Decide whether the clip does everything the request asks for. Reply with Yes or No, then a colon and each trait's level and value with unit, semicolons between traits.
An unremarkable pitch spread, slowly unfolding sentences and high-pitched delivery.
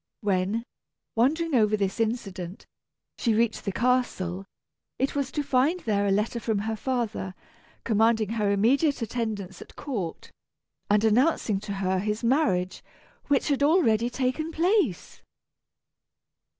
Yes: average, 4.5 semitones; slow, 130 wpm; high, 225 Hz